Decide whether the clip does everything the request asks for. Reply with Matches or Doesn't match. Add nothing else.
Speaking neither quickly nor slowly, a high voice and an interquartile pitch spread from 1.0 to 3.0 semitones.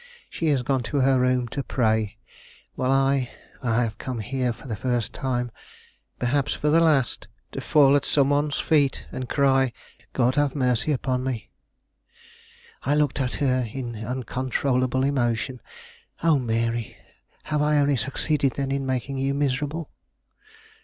Doesn't match